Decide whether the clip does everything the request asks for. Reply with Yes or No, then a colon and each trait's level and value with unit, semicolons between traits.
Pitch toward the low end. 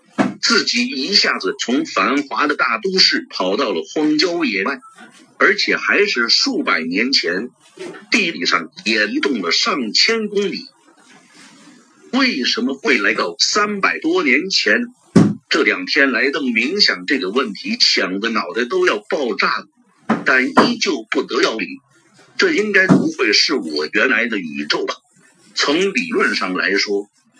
No: very high, 270 Hz